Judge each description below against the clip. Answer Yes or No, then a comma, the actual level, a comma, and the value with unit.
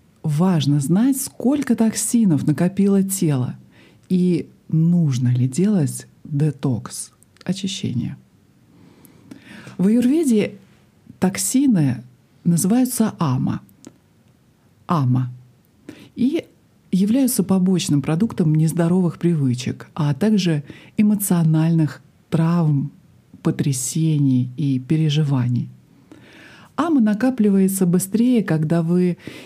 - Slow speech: Yes, slow, 75 wpm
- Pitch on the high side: No, medium, 170 Hz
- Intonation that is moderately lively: No, wide, 5.9 semitones